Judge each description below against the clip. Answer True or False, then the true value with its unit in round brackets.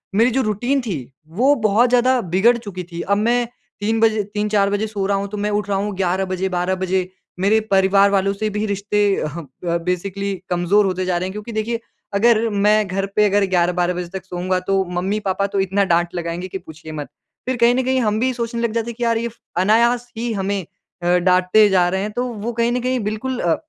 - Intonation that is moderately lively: True (3.5 semitones)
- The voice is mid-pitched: False (200 Hz)